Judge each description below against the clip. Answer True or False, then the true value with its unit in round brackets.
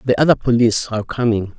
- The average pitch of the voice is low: True (115 Hz)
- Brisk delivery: False (190 wpm)